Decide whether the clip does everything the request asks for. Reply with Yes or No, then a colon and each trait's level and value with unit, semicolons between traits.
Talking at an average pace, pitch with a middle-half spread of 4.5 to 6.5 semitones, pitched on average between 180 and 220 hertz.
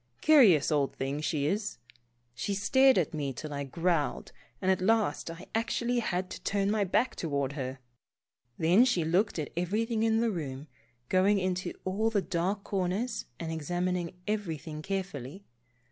Yes: average, 160 wpm; average, 5.1 semitones; medium, 185 Hz